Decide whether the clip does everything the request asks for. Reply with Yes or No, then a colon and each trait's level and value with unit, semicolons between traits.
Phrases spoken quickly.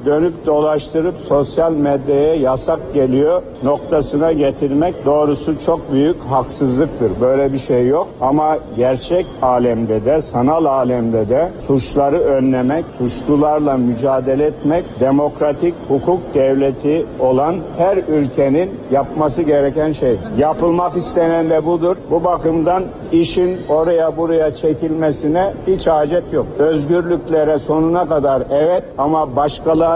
No: average, 110 wpm